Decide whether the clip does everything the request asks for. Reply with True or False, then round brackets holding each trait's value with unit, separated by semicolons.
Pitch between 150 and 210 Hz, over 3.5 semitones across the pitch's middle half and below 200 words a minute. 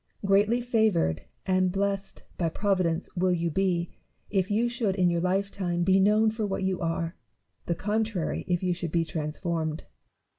False (185 Hz; 2.8 semitones; 160 wpm)